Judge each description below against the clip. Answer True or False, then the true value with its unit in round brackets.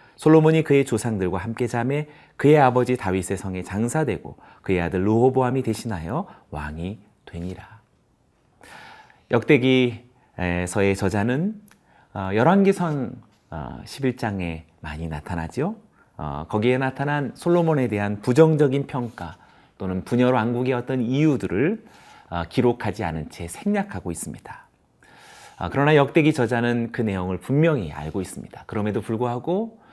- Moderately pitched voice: False (120 Hz)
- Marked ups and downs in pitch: True (6.6 semitones)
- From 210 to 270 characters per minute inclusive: False (285 characters per minute)